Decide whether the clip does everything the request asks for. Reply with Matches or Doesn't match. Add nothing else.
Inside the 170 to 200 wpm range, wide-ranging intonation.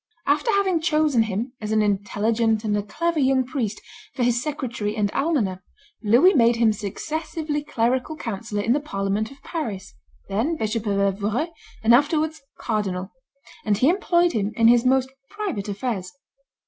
Doesn't match